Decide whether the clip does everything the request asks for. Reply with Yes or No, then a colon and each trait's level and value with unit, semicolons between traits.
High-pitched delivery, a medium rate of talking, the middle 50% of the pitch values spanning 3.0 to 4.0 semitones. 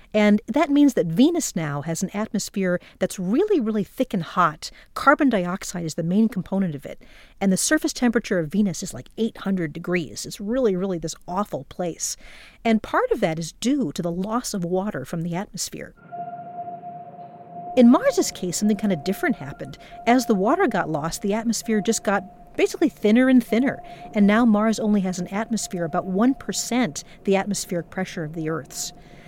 No: high, 200 Hz; average, 180 wpm; average, 4.8 semitones